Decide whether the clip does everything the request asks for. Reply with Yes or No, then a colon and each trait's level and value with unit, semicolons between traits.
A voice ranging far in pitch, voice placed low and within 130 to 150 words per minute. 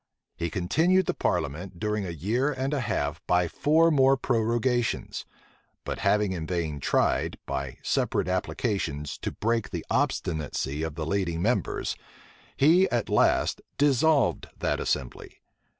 Yes: wide, 8.0 semitones; low, 105 Hz; slow, 135 wpm